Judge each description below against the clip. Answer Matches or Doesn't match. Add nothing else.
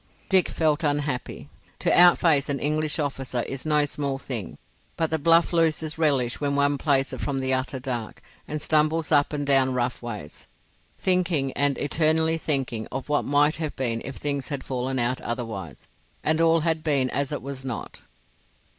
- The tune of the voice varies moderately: Matches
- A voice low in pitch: Doesn't match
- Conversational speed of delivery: Matches